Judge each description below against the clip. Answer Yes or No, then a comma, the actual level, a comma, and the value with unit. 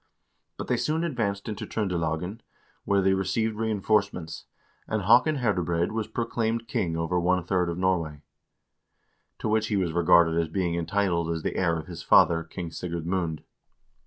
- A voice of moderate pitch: No, very low, 90 Hz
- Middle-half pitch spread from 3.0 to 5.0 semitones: Yes, average, 4.2 semitones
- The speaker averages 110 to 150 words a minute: No, average, 165 wpm